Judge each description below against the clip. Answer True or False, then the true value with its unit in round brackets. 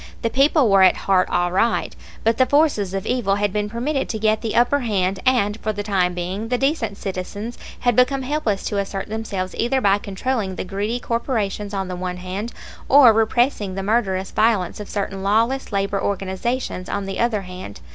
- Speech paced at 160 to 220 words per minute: True (195 wpm)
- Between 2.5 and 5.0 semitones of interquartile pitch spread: True (3.7 semitones)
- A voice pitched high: True (205 Hz)